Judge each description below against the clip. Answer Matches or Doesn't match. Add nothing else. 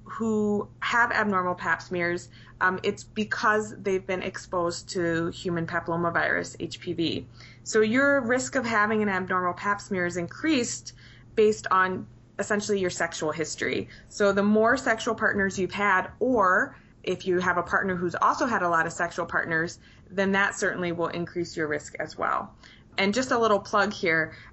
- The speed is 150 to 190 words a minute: Matches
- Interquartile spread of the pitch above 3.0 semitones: Matches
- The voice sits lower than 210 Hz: Matches